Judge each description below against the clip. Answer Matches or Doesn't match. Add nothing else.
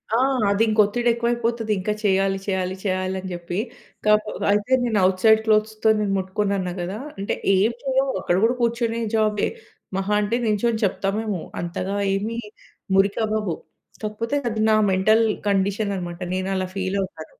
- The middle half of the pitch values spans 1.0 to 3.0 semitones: Matches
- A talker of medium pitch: Doesn't match